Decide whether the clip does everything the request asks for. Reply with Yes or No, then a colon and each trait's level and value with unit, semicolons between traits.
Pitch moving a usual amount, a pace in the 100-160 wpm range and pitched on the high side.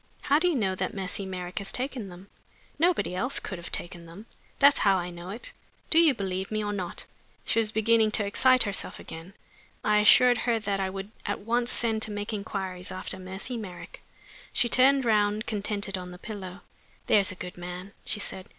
No: average, 3.5 semitones; average, 200 wpm; high, 205 Hz